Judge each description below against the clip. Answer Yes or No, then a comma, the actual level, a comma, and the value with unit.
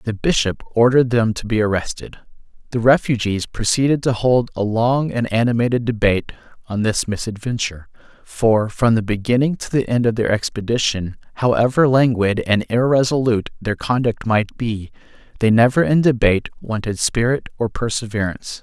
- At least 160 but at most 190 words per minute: No, average, 150 wpm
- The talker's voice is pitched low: Yes, low, 115 Hz